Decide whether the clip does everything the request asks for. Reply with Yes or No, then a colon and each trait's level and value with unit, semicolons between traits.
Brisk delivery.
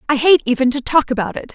Yes: fast, 270 wpm